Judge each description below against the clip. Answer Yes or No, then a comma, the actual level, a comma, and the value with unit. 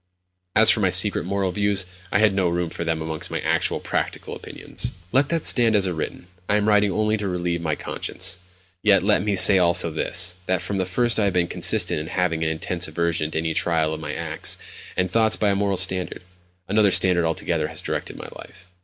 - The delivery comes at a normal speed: No, fast, 215 wpm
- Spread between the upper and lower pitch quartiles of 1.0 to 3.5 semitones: Yes, average, 3.1 semitones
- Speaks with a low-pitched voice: Yes, very low, 90 Hz